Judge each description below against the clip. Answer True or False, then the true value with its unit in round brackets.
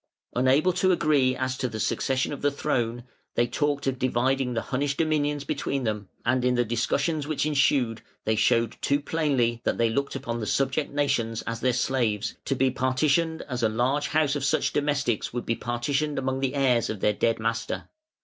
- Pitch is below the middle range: True (130 Hz)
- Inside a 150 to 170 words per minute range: False (195 wpm)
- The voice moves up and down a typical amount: True (3.4 semitones)